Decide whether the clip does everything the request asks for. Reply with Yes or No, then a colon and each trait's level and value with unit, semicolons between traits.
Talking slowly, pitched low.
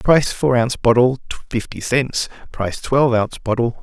Yes: slow, 125 wpm; low, 120 Hz